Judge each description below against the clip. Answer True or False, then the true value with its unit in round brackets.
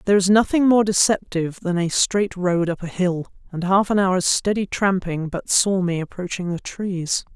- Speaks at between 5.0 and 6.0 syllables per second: False (4.8 syllables/s)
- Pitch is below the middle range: False (185 Hz)